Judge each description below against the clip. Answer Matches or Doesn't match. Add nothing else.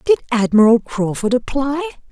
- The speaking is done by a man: Doesn't match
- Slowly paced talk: Matches